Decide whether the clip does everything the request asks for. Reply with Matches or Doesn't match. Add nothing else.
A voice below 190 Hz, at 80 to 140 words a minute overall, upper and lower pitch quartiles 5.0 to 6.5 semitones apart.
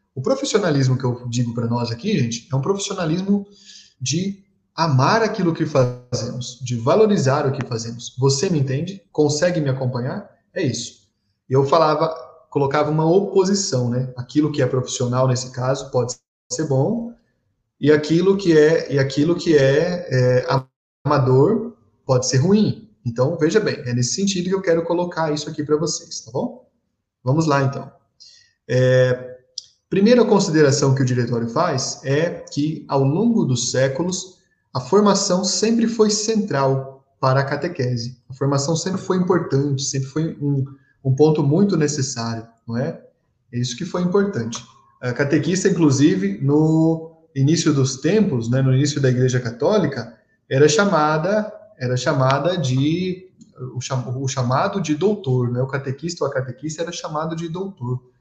Doesn't match